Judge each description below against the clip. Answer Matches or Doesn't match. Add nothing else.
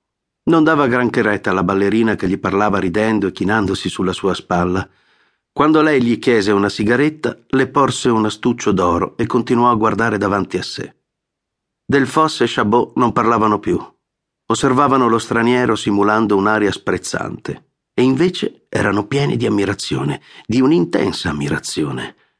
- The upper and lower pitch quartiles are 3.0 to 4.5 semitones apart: Matches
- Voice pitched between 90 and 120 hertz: Matches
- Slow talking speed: Doesn't match